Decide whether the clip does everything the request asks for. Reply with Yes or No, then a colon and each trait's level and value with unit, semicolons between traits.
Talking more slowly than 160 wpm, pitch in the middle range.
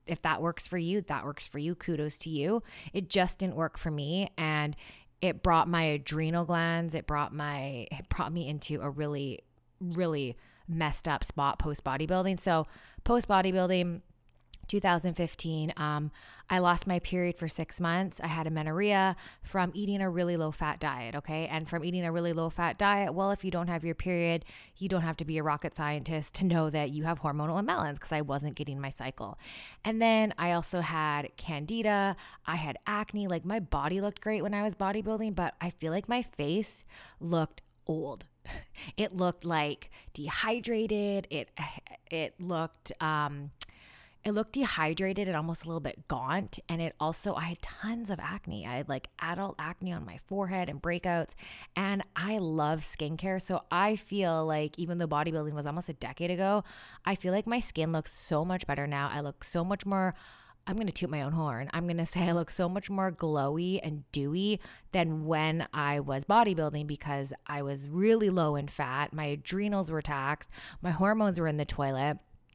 No: average, 190 wpm; medium, 165 Hz